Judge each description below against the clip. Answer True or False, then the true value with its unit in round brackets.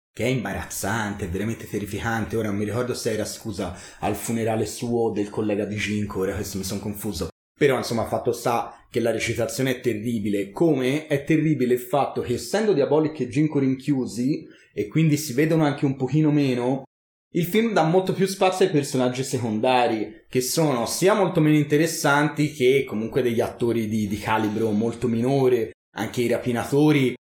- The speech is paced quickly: True (175 wpm)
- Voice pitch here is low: True (125 Hz)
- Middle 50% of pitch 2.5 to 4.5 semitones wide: False (5.0 semitones)